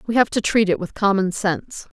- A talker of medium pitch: No, high, 200 Hz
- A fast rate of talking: Yes, fast, 240 wpm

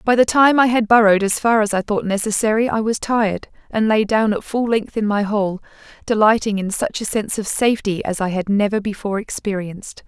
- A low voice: No, high, 215 Hz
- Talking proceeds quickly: Yes, fast, 220 wpm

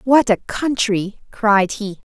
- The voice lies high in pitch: Yes, high, 215 Hz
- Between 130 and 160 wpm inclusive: Yes, average, 140 wpm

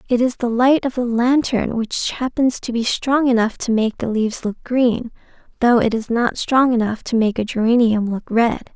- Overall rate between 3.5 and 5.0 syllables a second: Yes, 4.7 syllables/s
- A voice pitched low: No, high, 235 Hz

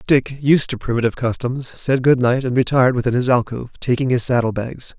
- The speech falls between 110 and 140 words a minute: No, fast, 205 wpm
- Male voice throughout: Yes, male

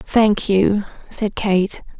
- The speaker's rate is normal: No, slow, 120 wpm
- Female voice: Yes, female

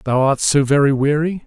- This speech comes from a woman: No, male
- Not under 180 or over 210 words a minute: Yes, fast, 205 wpm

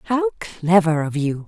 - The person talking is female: Yes, female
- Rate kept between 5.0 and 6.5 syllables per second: No, 4.3 syllables/s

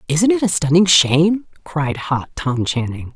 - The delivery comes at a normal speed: Yes, average, 170 wpm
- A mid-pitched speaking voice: Yes, medium, 160 Hz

